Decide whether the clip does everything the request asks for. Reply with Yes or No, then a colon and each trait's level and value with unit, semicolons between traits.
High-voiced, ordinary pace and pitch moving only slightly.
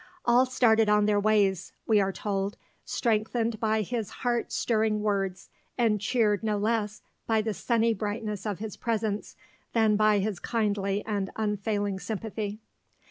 Yes: high, 215 Hz; average, 145 wpm; narrow, 1.5 semitones